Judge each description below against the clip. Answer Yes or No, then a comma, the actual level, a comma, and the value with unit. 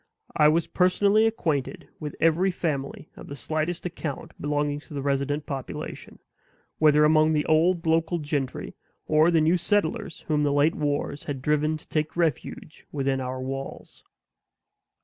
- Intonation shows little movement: Yes, narrow, 2.3 semitones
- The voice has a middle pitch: Yes, medium, 155 Hz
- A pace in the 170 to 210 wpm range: No, average, 150 wpm